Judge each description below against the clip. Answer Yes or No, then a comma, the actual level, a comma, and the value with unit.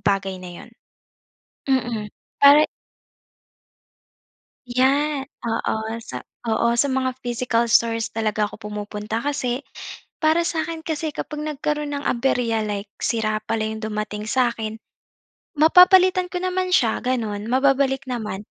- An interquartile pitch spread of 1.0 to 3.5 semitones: No, average, 4.9 semitones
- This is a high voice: Yes, high, 240 Hz